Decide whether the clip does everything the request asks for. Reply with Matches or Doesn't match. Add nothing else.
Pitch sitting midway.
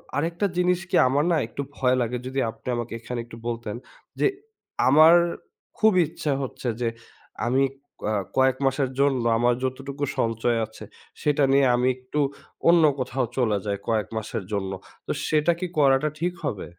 Doesn't match